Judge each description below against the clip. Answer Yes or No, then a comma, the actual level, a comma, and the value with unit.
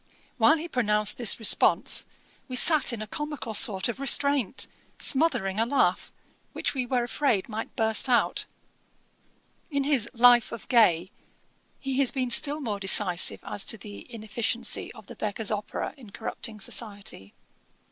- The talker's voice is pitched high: Yes, high, 235 Hz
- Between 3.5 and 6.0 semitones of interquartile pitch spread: Yes, average, 4.1 semitones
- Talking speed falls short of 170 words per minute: Yes, average, 150 wpm